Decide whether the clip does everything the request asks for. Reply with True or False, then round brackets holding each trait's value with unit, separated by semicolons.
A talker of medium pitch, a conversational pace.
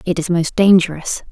True (175 Hz; 185 wpm)